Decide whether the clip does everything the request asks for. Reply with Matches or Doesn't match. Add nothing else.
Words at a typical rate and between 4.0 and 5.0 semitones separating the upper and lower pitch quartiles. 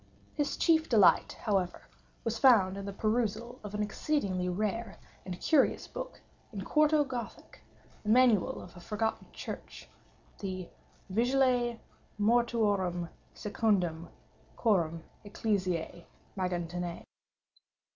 Doesn't match